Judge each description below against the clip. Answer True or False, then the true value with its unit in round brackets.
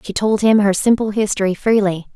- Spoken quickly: False (195 wpm)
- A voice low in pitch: False (205 Hz)